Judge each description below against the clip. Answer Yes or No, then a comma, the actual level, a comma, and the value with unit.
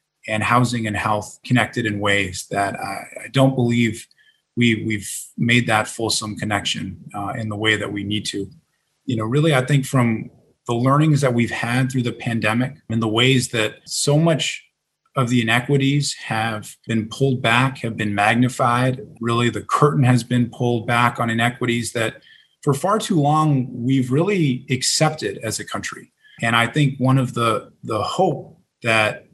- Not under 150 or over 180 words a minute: Yes, average, 175 wpm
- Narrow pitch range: No, average, 3.0 semitones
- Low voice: Yes, low, 120 Hz